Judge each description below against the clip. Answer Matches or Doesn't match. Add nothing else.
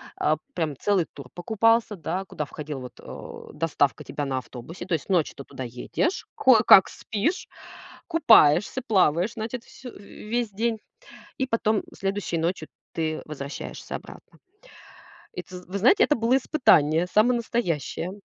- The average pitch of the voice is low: Doesn't match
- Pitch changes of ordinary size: Doesn't match